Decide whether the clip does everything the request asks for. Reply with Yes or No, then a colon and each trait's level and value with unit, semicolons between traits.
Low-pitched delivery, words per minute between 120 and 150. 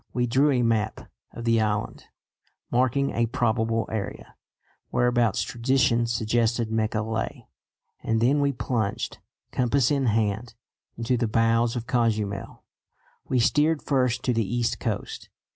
Yes: low, 115 Hz; slow, 135 wpm